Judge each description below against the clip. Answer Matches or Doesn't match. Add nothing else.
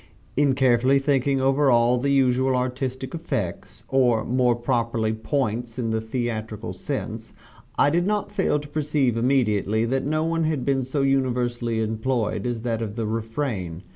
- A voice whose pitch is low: Matches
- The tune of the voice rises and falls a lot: Doesn't match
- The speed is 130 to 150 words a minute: Doesn't match